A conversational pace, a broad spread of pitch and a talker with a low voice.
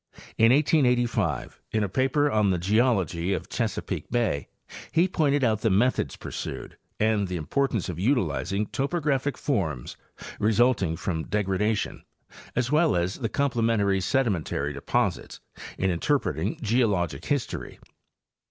No: slow, 130 wpm; wide, 5.8 semitones; low, 110 Hz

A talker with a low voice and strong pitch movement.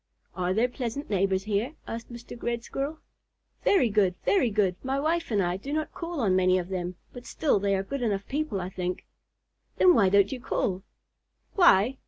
No: high, 220 Hz; wide, 6.2 semitones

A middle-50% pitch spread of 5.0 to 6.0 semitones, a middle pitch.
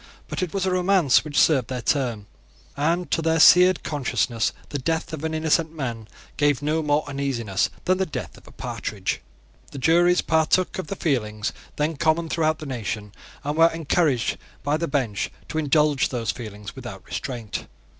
No: average, 4.6 semitones; medium, 150 Hz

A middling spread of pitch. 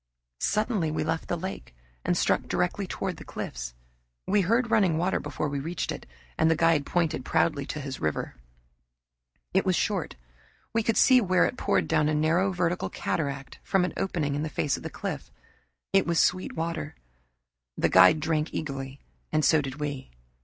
Yes: average, 4.2 semitones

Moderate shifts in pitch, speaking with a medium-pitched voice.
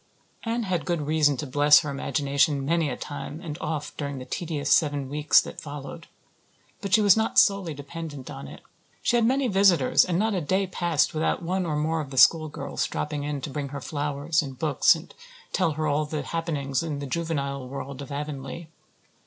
Yes: average, 3.0 semitones; medium, 150 Hz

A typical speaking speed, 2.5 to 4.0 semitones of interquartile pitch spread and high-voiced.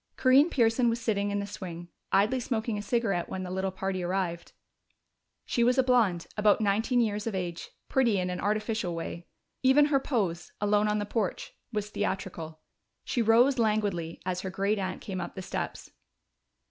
Yes: average, 180 wpm; average, 3.7 semitones; high, 205 Hz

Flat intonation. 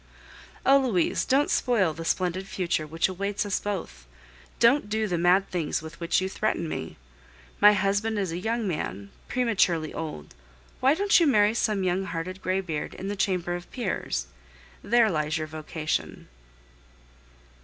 No: average, 4.6 semitones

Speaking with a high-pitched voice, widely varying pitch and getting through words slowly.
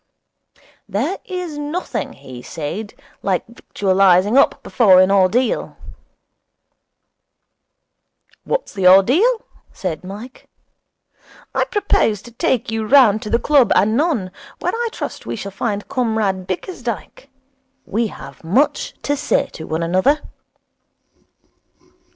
Yes: high, 220 Hz; wide, 6.5 semitones; slow, 115 wpm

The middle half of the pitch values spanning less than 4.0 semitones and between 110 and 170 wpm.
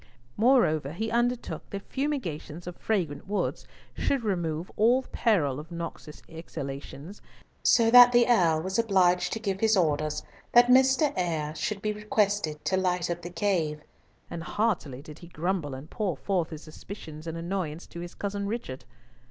No: wide, 5.6 semitones; average, 160 wpm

